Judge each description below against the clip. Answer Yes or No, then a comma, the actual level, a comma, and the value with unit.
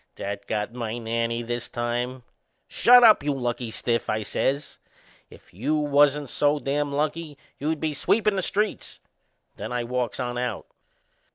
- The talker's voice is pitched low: Yes, low, 125 Hz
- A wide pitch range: No, average, 3.8 semitones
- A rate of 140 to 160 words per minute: Yes, average, 155 wpm